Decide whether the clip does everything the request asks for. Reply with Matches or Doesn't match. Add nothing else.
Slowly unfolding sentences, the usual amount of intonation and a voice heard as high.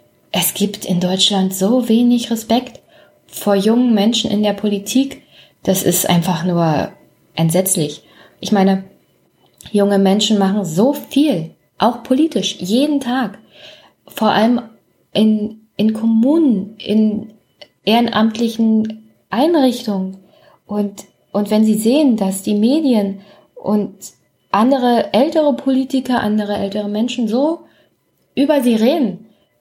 Matches